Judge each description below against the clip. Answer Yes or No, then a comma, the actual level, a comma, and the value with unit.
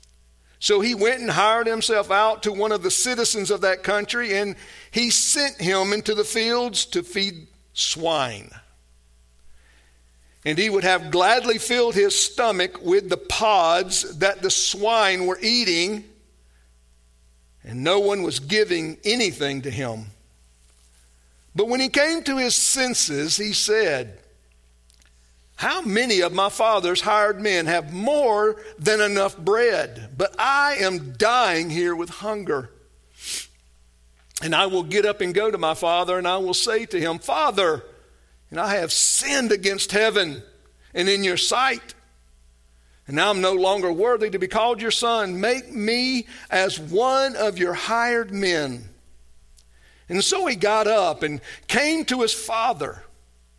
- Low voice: No, high, 190 Hz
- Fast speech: No, average, 150 wpm